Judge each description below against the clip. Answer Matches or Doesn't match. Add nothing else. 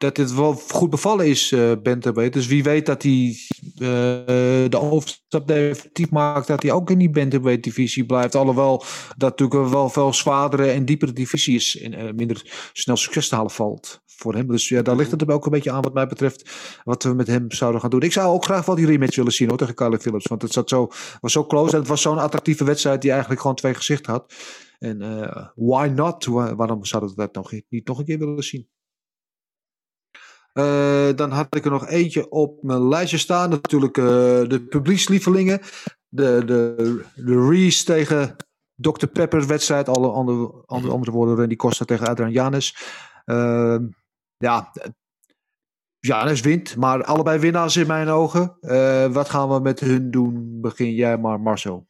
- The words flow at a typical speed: Matches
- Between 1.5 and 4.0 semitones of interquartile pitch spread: Matches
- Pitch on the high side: Doesn't match